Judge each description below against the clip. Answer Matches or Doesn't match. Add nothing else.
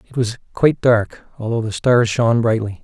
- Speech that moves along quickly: Doesn't match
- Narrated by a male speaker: Matches